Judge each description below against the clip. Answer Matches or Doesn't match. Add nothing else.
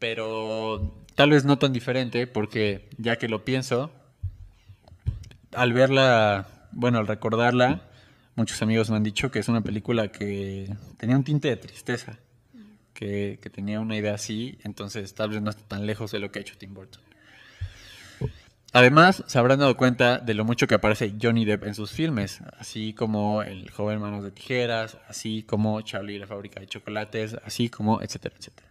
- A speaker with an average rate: Matches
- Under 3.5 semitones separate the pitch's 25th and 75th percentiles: Matches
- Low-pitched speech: Matches